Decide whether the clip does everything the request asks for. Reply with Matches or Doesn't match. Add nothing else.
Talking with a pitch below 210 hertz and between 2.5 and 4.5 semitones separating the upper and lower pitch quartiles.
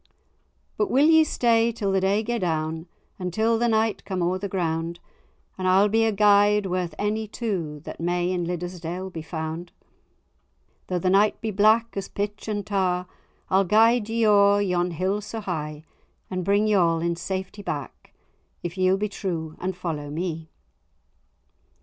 Matches